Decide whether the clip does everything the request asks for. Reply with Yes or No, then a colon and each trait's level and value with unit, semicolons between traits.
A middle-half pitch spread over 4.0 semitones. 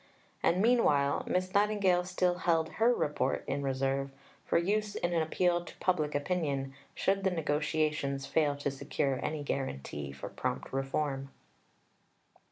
Yes: average, 4.8 semitones